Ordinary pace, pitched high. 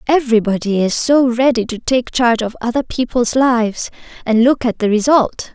Yes: average, 175 wpm; high, 240 Hz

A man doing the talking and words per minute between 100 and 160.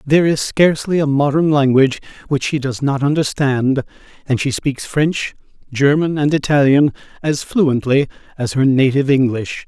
Yes: male; average, 150 wpm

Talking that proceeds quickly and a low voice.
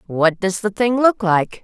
No: fast, 220 wpm; high, 200 Hz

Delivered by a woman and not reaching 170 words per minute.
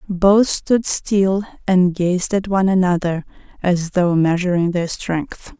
Yes: female; average, 140 wpm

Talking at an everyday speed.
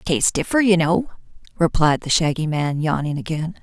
Yes: average, 165 wpm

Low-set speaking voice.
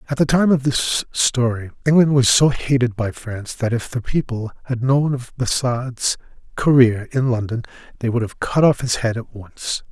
Yes: low, 125 Hz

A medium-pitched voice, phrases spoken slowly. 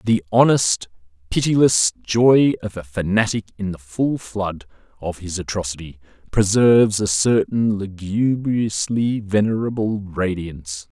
No: low, 100 Hz; slow, 110 wpm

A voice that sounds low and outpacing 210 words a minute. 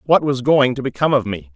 Yes: low, 130 Hz; fast, 270 wpm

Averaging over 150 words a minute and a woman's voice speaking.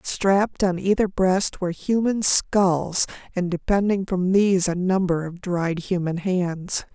No: average, 145 wpm; female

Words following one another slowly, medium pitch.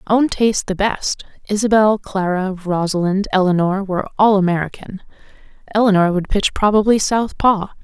No: slow, 125 wpm; high, 200 Hz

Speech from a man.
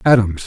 Yes: male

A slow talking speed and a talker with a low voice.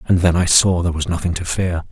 No: fast, 280 wpm; very low, 85 Hz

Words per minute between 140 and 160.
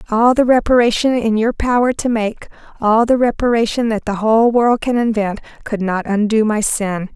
No: average, 175 wpm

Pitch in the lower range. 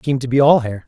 Yes: low, 130 Hz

